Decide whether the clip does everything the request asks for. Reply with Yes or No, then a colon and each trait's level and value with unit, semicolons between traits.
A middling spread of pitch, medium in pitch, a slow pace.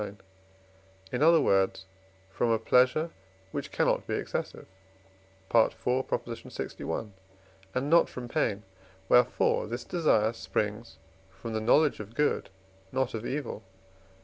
No: average, 3.5 semitones; low, 120 Hz; slow, 125 wpm